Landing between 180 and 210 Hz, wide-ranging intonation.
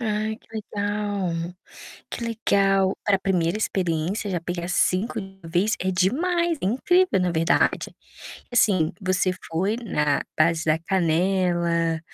No: high, 190 Hz; average, 3.7 semitones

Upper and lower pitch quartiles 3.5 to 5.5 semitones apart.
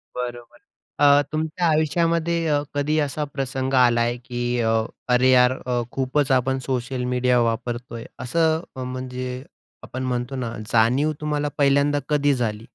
No: average, 2.9 semitones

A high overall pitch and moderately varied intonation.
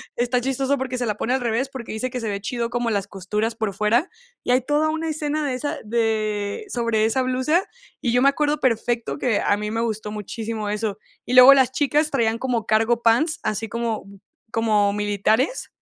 Yes: high, 235 Hz; average, 3.4 semitones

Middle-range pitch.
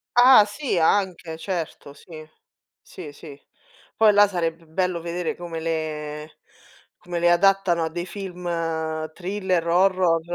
Yes: medium, 175 Hz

